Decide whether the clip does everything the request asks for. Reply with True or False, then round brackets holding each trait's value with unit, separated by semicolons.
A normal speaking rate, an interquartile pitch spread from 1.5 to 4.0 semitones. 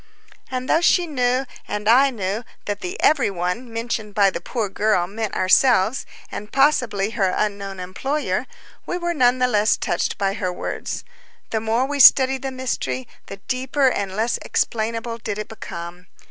False (170 wpm; 4.6 semitones)